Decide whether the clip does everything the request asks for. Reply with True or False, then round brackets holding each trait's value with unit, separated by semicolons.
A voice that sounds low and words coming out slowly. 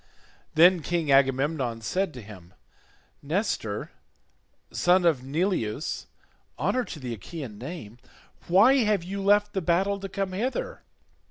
False (170 Hz; 125 wpm)